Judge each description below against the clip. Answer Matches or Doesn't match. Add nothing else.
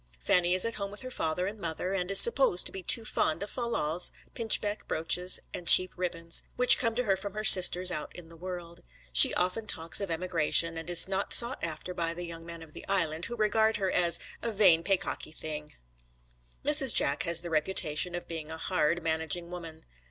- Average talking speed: Doesn't match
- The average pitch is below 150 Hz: Doesn't match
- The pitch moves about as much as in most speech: Matches